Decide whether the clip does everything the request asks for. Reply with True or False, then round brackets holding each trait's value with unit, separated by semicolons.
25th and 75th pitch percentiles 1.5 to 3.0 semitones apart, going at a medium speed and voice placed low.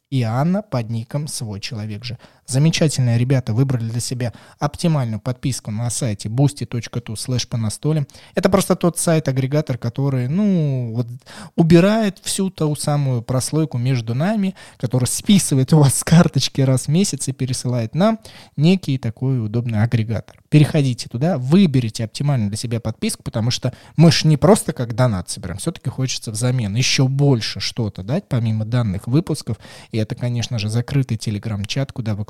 False (4.4 semitones; 150 wpm; 130 Hz)